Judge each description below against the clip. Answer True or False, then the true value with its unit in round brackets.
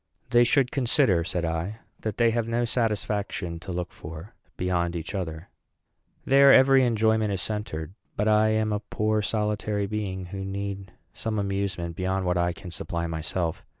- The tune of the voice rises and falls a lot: False (3.8 semitones)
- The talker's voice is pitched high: False (100 Hz)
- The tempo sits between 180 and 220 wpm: False (165 wpm)